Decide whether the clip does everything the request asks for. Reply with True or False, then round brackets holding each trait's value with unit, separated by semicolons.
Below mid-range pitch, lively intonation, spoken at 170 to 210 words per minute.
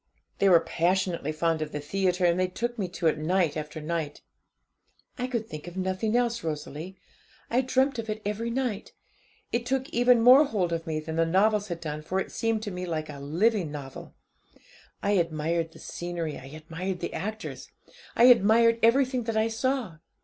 False (185 Hz; 5.8 semitones; 190 wpm)